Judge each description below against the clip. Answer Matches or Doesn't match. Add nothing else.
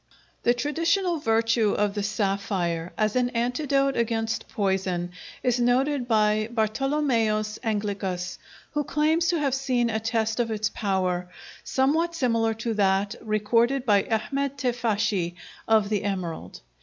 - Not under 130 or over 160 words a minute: Matches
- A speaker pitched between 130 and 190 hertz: Doesn't match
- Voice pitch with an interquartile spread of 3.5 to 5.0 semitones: Matches